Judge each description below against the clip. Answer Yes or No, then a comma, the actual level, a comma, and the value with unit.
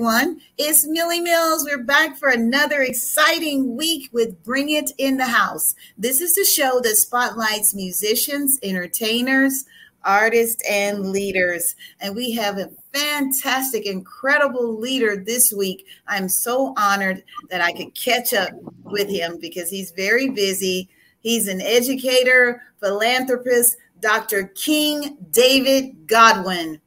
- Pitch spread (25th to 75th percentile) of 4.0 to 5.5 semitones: Yes, average, 5.2 semitones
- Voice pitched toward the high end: Yes, high, 240 Hz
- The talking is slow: Yes, slow, 125 wpm